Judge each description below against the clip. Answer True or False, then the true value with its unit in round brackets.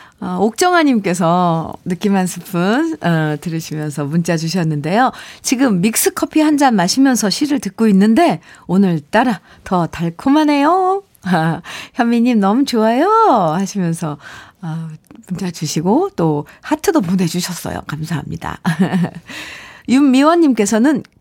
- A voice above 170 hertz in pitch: True (190 Hz)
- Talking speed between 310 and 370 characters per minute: False (270 characters per minute)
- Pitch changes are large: True (7.6 semitones)